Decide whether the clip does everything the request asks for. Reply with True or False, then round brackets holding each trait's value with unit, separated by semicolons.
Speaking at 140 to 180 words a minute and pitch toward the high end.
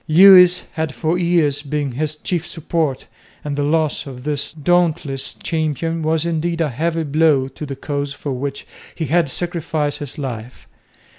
False (160 wpm; 155 Hz)